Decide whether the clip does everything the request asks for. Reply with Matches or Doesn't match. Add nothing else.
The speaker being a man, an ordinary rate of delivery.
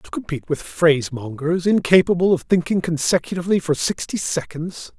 Doesn't match